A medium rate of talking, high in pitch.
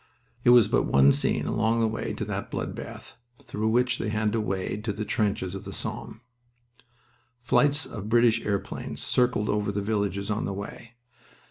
No: average, 185 wpm; low, 105 Hz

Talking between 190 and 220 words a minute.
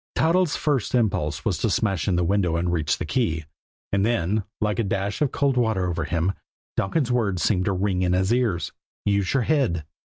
Yes: average, 200 wpm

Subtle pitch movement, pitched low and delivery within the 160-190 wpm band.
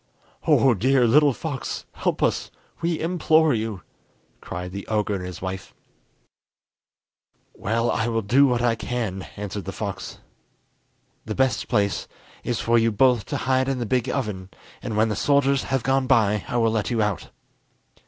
No: average, 4.1 semitones; low, 115 Hz; average, 165 wpm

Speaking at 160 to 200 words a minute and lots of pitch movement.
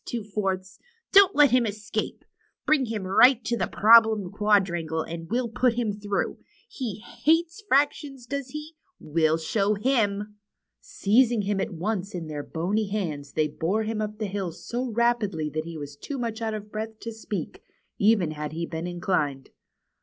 No: average, 175 wpm; average, 5.0 semitones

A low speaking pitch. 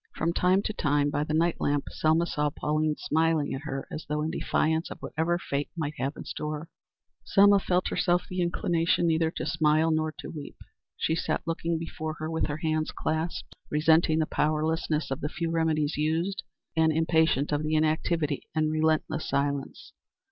No: medium, 155 Hz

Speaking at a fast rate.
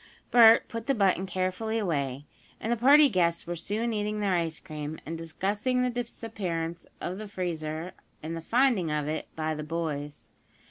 No: average, 175 wpm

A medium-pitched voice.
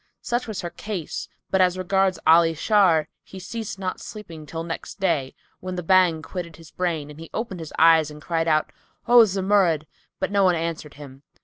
Yes: medium, 175 Hz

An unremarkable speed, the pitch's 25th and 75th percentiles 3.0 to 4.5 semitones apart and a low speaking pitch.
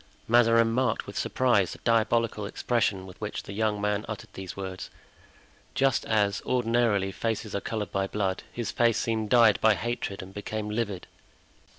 No: average, 165 wpm; narrow, 2.6 semitones; low, 110 Hz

